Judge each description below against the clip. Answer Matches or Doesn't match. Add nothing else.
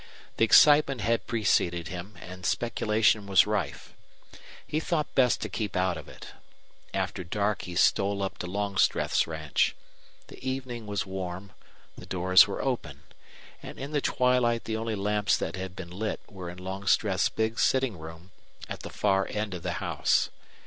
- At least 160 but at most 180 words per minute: Matches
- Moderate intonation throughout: Matches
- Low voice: Matches